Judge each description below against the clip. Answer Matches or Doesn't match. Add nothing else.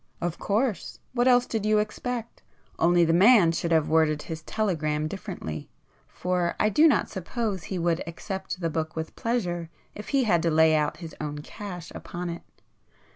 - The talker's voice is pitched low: Doesn't match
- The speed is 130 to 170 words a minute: Doesn't match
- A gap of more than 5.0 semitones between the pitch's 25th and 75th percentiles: Doesn't match